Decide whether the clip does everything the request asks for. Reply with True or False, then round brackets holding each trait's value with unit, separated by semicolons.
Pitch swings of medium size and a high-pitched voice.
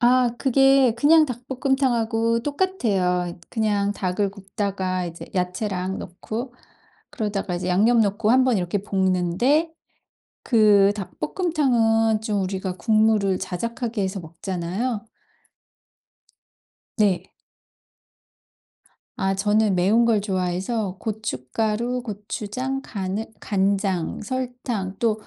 True (4.0 semitones; 210 Hz)